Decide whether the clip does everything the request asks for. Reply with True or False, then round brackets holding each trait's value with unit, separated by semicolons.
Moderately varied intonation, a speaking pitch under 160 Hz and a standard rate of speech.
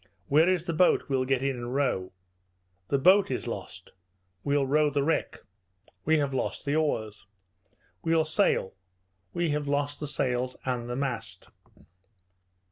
True (3.4 semitones; 140 Hz; 150 wpm)